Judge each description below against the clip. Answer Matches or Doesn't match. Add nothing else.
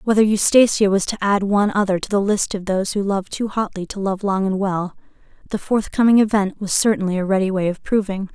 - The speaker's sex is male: Doesn't match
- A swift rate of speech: Matches